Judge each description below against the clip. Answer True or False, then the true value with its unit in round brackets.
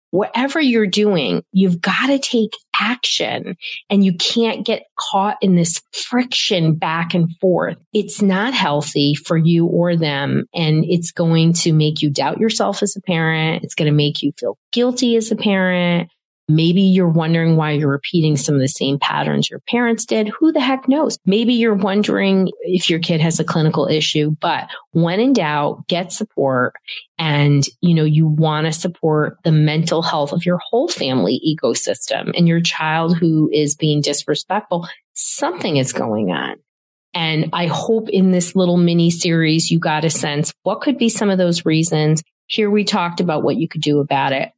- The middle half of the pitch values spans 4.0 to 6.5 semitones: True (4.3 semitones)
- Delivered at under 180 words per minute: False (185 wpm)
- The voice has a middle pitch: True (170 Hz)